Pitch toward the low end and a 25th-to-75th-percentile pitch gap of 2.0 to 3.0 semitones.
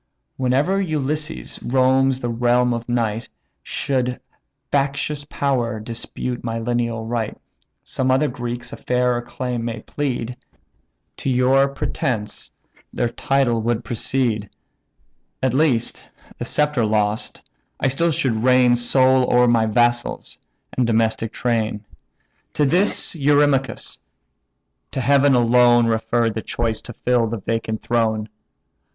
Yes: low, 120 Hz; narrow, 2.5 semitones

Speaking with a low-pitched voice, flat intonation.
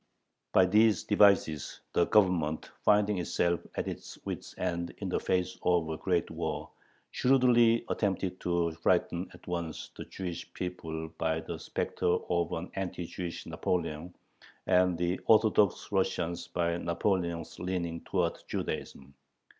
Yes: very low, 90 Hz; narrow, 2.1 semitones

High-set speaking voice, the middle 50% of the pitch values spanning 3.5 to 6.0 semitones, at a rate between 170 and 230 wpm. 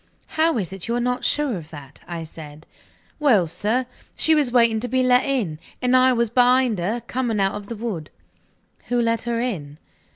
Yes: high, 235 Hz; average, 5.1 semitones; average, 200 wpm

